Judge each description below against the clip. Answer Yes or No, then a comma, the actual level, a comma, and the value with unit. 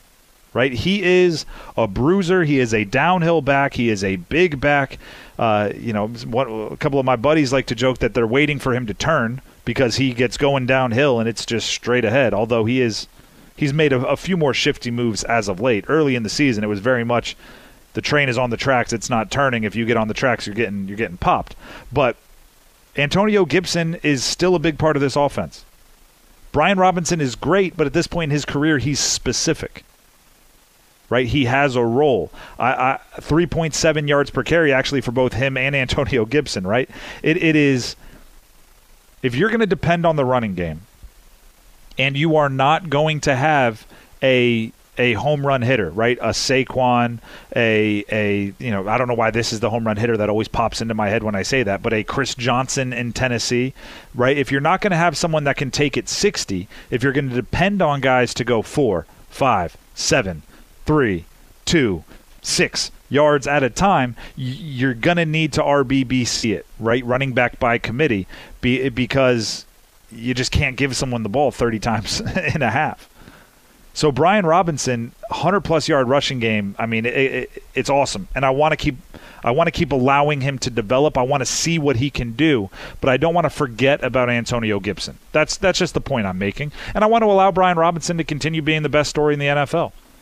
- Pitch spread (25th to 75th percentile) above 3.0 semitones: Yes, average, 4.2 semitones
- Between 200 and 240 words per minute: Yes, fast, 205 wpm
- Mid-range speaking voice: No, low, 130 Hz